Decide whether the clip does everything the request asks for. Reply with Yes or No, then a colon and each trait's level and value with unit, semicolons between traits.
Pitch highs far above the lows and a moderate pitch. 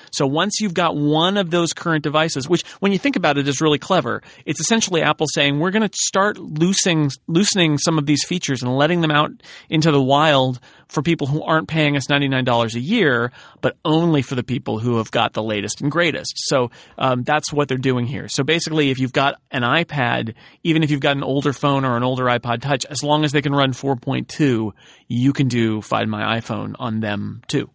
No: average, 3.9 semitones; medium, 145 Hz